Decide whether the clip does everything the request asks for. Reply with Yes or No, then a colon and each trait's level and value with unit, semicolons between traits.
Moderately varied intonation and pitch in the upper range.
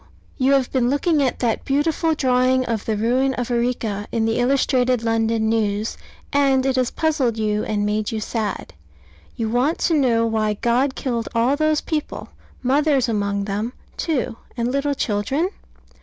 Yes: average, 3.5 semitones; high, 245 Hz